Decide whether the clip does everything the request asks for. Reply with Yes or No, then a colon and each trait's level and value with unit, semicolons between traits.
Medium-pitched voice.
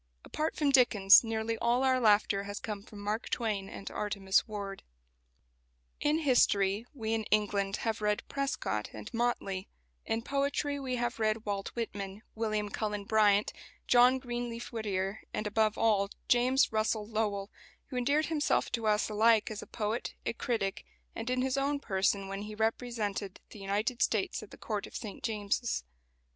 No: high, 220 Hz